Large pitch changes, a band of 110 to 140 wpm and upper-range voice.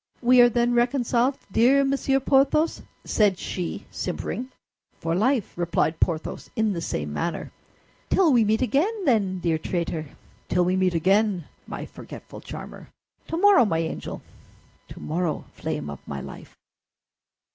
Yes: wide, 7.1 semitones; slow, 135 wpm; high, 215 Hz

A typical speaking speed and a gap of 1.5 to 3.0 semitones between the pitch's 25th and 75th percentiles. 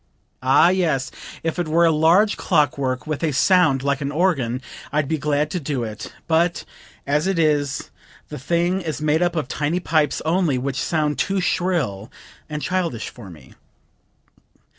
No: average, 170 wpm; average, 3.7 semitones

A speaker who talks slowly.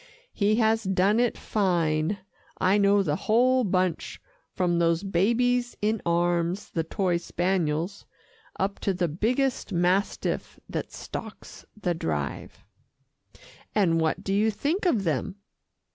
Yes: slow, 130 wpm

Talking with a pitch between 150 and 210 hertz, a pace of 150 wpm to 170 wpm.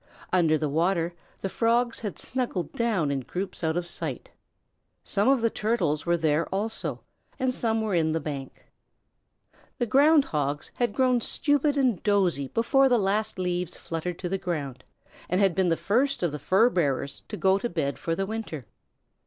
No: high, 190 Hz; average, 180 wpm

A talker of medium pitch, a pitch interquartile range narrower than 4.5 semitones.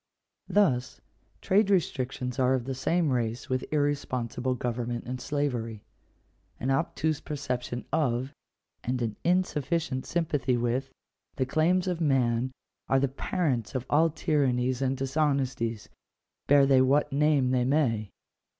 No: low, 130 Hz; average, 3.3 semitones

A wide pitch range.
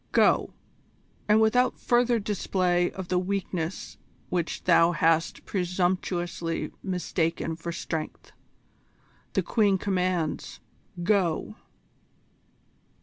No: average, 2.7 semitones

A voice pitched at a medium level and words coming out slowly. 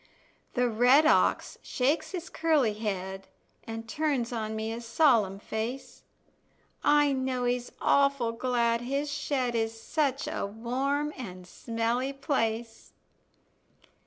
No: high, 245 Hz; slow, 120 wpm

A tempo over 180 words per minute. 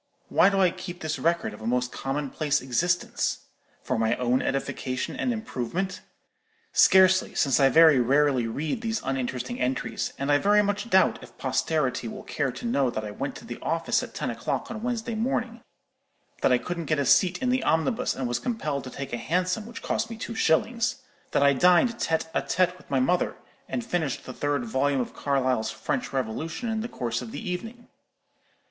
Yes: average, 195 wpm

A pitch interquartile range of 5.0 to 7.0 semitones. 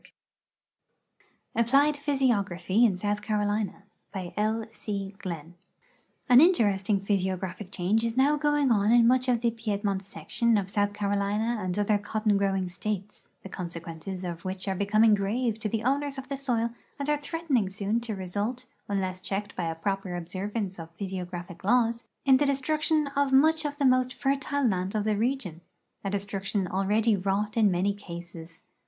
No: average, 4.0 semitones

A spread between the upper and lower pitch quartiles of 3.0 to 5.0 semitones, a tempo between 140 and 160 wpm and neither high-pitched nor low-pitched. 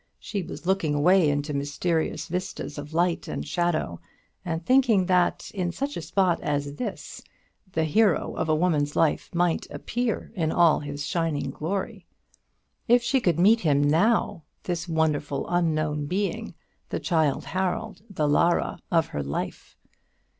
Yes: average, 3.9 semitones; average, 150 wpm; medium, 165 Hz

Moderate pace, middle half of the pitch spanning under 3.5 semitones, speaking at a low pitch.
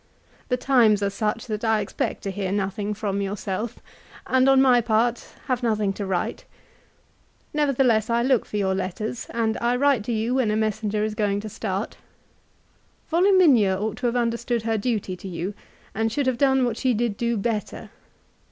No: average, 180 wpm; average, 3.0 semitones; high, 220 Hz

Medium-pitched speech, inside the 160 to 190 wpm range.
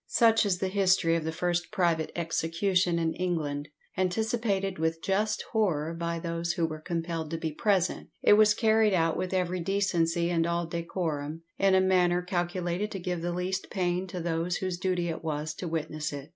Yes: medium, 175 Hz; average, 185 wpm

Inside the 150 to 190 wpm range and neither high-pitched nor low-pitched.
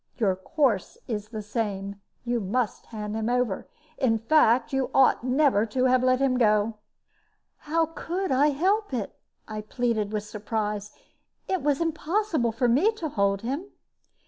No: average, 155 wpm; high, 245 Hz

